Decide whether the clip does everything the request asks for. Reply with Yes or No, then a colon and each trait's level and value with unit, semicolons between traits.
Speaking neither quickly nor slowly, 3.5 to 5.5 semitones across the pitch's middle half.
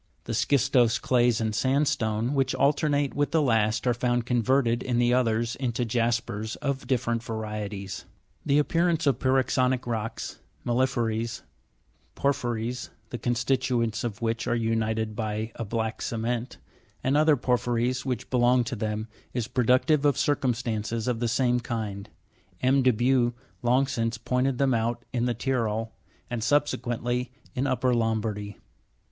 No: average, 145 wpm; narrow, 2.5 semitones